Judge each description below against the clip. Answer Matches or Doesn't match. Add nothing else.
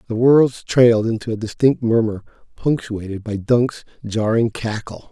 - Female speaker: Doesn't match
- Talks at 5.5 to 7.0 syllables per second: Doesn't match